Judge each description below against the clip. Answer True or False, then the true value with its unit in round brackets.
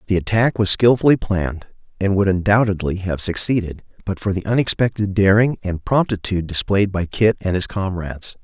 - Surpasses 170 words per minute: False (165 wpm)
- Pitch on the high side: False (100 Hz)